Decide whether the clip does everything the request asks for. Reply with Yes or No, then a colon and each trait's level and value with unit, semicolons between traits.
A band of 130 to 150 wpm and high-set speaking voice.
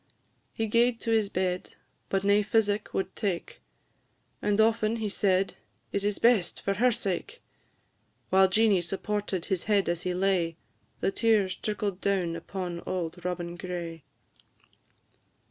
Yes: average, 140 wpm; high, 195 Hz